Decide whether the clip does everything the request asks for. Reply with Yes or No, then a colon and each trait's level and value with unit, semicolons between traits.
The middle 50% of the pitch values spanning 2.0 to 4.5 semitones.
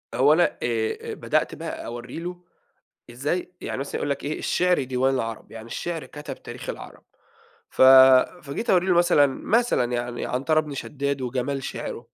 No: wide, 5.4 semitones